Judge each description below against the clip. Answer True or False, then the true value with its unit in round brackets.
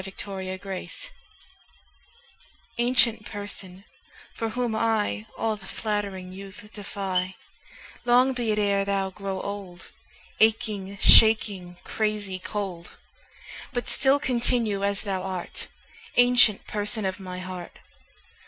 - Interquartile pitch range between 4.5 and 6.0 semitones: False (2.8 semitones)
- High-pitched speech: True (200 Hz)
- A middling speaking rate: False (110 wpm)